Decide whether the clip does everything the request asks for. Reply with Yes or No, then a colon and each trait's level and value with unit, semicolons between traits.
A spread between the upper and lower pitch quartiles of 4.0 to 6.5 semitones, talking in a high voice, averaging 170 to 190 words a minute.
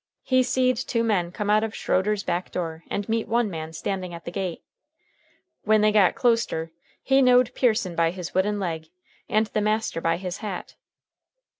Yes: average, 4.3 semitones; high, 205 Hz; average, 180 wpm